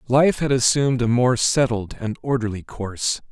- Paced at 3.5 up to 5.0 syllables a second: Yes, 4.9 syllables/s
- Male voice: Yes, male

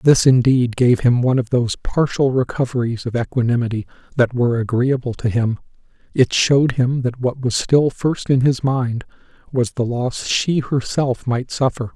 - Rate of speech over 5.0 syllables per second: No, 4.8 syllables/s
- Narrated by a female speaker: No, male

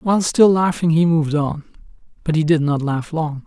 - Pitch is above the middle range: No, medium, 160 Hz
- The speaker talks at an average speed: No, fast, 210 wpm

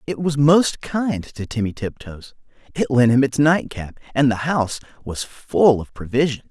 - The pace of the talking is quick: No, average, 175 wpm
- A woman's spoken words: No, male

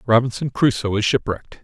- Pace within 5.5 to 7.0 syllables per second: Yes, 6.0 syllables/s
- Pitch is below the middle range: Yes, low, 115 Hz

